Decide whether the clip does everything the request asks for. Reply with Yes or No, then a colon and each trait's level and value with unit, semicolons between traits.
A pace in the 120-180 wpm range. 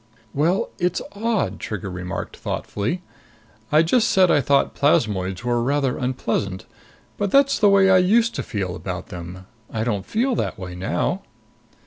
Yes: average, 155 wpm